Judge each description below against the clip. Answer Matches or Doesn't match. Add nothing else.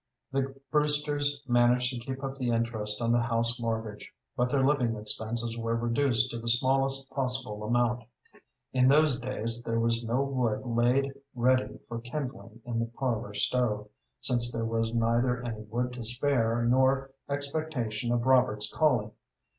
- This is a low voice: Matches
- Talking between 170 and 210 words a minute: Doesn't match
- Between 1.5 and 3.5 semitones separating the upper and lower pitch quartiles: Matches